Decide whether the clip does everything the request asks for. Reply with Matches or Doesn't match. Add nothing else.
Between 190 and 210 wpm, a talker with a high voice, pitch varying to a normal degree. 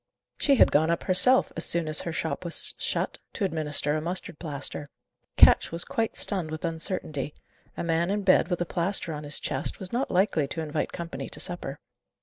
Doesn't match